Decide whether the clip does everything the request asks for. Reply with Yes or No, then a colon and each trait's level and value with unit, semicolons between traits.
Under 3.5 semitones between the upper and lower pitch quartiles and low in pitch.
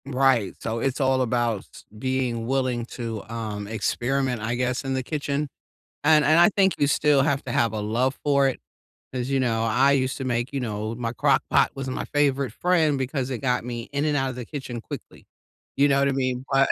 Yes: narrow, 2.6 semitones; low, 130 Hz